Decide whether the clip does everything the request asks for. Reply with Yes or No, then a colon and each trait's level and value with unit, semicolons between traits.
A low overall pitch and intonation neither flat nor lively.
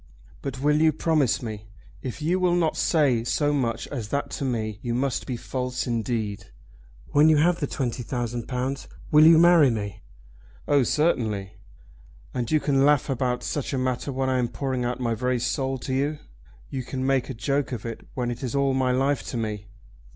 Yes: low, 130 Hz; average, 3.1 semitones